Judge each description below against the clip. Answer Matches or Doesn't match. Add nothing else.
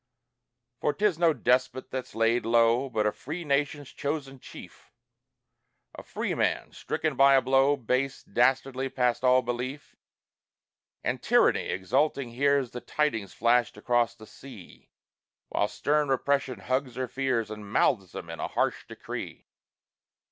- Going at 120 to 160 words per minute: Matches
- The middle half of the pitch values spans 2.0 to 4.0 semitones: Matches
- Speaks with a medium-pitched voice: Doesn't match